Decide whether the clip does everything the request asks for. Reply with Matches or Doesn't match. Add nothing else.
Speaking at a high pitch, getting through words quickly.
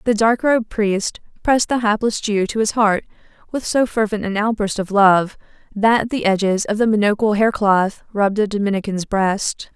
Doesn't match